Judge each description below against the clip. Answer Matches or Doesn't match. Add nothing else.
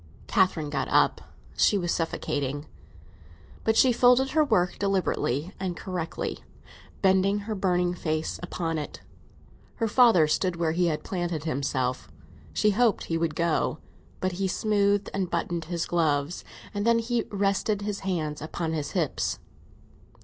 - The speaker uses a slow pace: Doesn't match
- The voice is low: Doesn't match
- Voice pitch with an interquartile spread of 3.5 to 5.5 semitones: Matches